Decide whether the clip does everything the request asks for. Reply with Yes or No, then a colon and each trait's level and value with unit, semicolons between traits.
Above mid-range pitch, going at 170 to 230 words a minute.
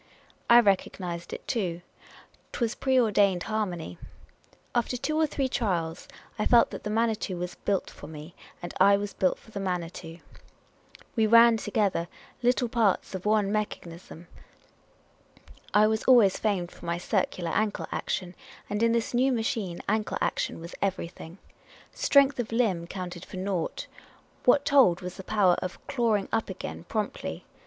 No: high, 205 Hz; average, 160 wpm